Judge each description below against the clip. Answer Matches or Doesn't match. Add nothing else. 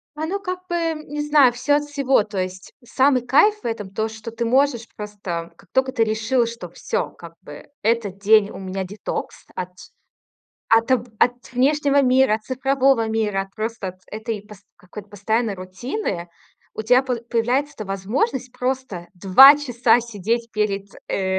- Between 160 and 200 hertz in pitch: Doesn't match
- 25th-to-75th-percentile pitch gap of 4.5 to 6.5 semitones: Matches